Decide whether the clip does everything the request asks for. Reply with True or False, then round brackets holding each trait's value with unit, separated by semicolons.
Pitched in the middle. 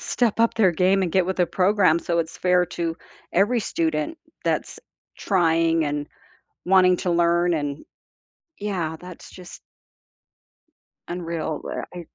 True (175 Hz)